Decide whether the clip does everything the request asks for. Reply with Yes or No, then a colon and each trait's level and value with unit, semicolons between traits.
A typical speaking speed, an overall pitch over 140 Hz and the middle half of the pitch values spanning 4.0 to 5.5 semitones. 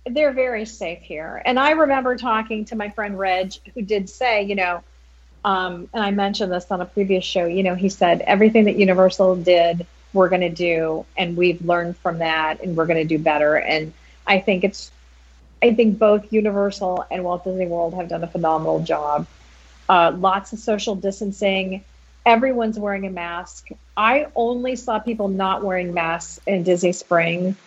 No: average, 185 wpm; high, 190 Hz; average, 3.6 semitones